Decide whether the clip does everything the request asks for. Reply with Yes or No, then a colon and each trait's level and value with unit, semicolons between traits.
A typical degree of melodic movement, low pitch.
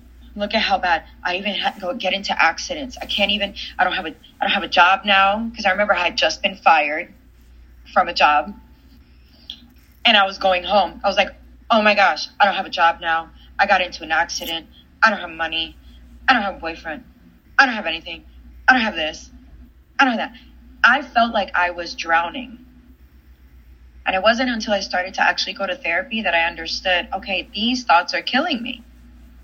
No: average, 4.3 semitones; medium, 180 Hz